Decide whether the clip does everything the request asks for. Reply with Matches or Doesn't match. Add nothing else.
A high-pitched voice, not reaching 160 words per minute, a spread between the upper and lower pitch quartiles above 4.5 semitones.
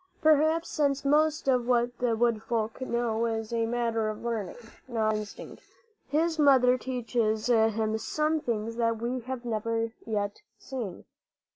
Doesn't match